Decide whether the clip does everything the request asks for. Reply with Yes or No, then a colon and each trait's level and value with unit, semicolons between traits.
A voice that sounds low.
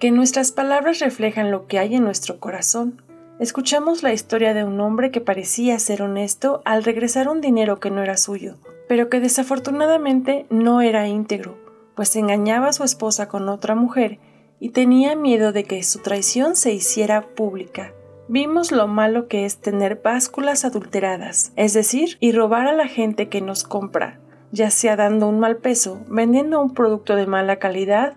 No: high, 220 Hz